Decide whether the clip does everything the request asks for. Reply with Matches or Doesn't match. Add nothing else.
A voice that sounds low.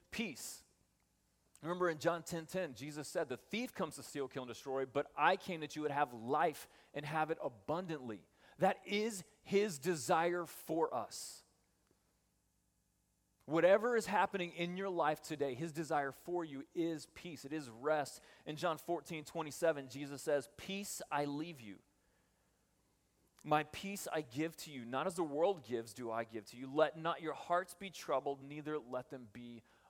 Doesn't match